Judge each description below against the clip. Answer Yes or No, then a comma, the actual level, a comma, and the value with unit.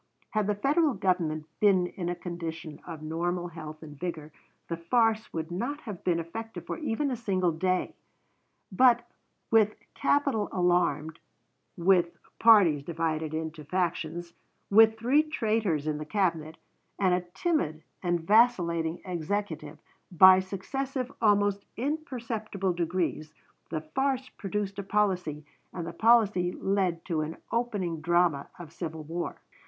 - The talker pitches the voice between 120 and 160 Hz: No, medium, 180 Hz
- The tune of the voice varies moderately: Yes, average, 4.8 semitones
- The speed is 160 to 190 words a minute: No, slow, 135 wpm